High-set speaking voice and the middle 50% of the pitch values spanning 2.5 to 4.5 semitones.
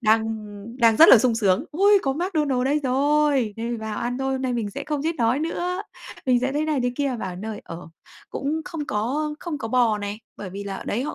No: very high, 250 Hz; average, 5.3 semitones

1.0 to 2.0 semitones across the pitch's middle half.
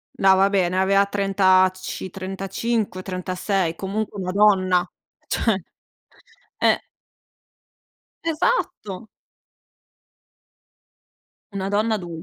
Yes: narrow, 1.6 semitones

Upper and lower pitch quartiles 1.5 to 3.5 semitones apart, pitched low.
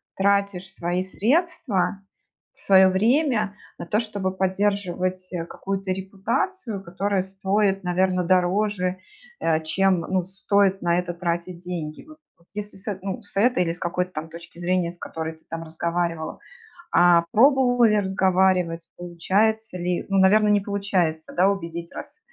No: narrow, 2.5 semitones; high, 190 Hz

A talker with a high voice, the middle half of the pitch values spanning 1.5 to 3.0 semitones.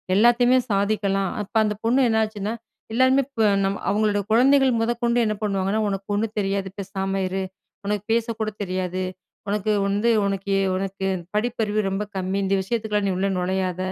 Yes: high, 205 Hz; average, 2.7 semitones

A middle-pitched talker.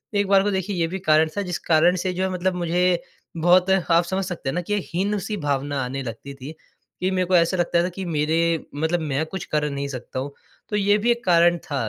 Yes: medium, 175 Hz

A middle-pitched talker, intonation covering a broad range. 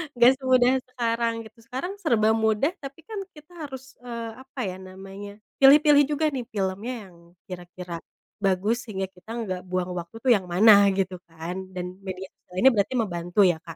No: high, 215 Hz; wide, 5.7 semitones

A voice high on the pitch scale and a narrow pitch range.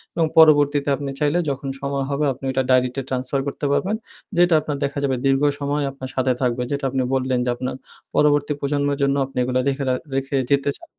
No: medium, 140 Hz; narrow, 1.6 semitones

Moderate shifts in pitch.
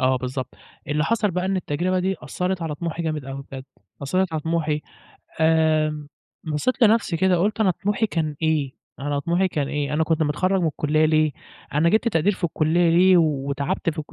Yes: average, 3.5 semitones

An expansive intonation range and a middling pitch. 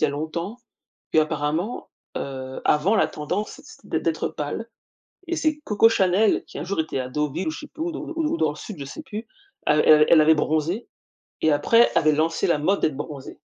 Yes: wide, 6.4 semitones; medium, 160 Hz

